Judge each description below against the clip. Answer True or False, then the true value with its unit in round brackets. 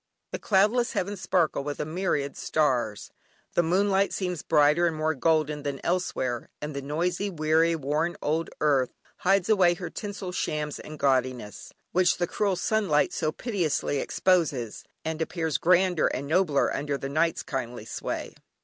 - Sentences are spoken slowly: False (150 wpm)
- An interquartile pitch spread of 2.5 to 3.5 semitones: False (3.9 semitones)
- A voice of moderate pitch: True (160 Hz)